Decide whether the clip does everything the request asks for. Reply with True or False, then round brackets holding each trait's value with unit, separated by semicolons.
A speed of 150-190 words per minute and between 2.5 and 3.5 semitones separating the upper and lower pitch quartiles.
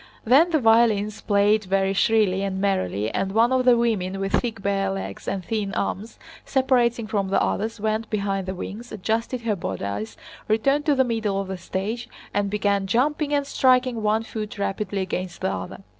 True (185 wpm; 3.2 semitones)